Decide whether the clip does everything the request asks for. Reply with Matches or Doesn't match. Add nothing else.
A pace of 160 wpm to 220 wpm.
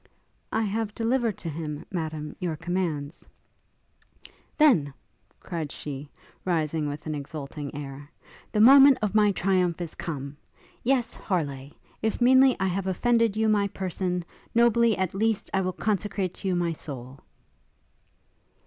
Doesn't match